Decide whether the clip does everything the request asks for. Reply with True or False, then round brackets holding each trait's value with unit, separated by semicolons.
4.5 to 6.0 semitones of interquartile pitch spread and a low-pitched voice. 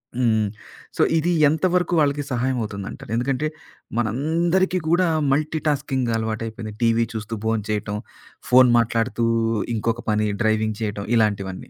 True (5.0 semitones; 115 Hz)